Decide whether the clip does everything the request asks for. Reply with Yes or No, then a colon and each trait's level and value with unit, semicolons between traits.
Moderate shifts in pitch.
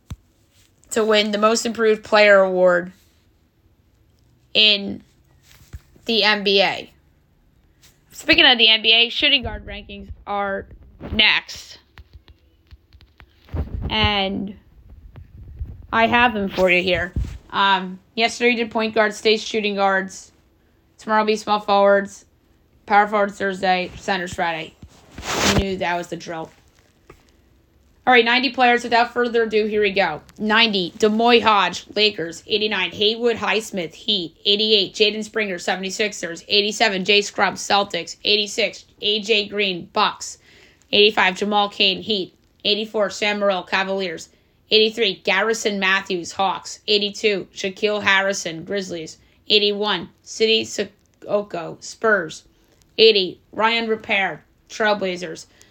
Yes: average, 3.6 semitones